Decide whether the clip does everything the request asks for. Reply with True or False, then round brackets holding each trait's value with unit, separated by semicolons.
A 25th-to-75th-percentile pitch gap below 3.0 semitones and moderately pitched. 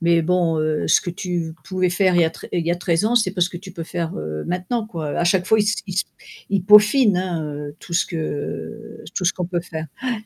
True (2.6 semitones; 180 Hz)